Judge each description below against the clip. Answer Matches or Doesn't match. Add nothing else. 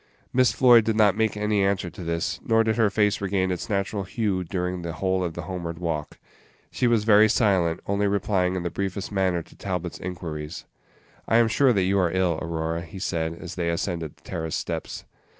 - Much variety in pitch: Doesn't match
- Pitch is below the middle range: Matches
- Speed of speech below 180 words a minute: Doesn't match